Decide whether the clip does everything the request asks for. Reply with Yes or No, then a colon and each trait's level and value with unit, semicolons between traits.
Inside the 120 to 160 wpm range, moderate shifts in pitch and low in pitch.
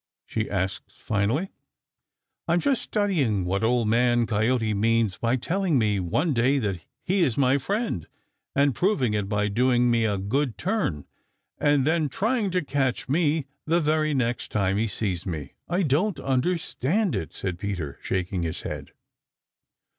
No: average, 155 wpm; wide, 7.4 semitones; low, 125 Hz